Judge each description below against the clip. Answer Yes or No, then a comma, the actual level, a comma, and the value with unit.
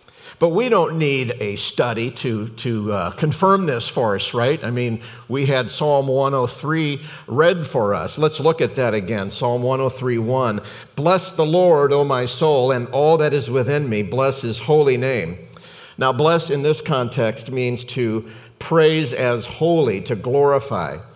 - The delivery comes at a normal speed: Yes, average, 165 wpm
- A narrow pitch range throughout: No, average, 4.1 semitones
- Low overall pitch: Yes, low, 130 Hz